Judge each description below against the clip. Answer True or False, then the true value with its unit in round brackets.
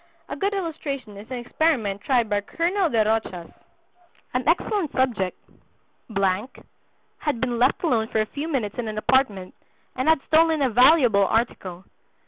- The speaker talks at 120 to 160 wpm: True (150 wpm)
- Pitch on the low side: False (250 Hz)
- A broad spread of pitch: True (6.5 semitones)